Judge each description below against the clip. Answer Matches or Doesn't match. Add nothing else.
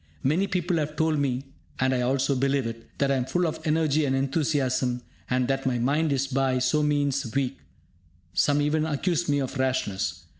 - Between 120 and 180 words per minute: Doesn't match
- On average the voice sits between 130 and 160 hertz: Matches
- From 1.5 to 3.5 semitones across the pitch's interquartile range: Matches